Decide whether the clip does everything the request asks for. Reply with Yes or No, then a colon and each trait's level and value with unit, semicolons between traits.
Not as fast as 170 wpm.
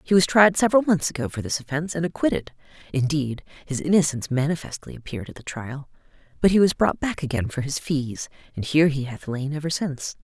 No: fast, 205 wpm